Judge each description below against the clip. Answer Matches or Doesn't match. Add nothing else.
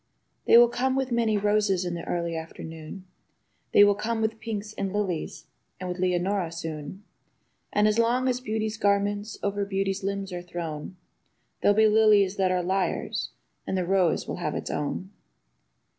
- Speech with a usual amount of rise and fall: Matches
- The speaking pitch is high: Matches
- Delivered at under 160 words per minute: Doesn't match